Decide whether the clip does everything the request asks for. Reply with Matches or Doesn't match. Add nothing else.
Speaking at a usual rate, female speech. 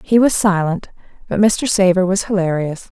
Matches